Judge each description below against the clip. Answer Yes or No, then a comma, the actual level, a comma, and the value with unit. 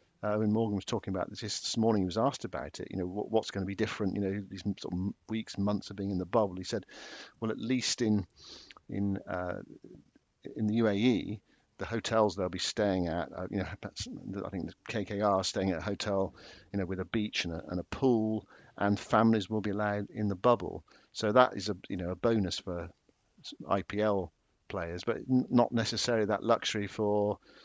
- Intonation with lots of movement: No, narrow, 2.5 semitones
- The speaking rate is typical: No, fast, 215 wpm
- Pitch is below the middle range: Yes, low, 105 Hz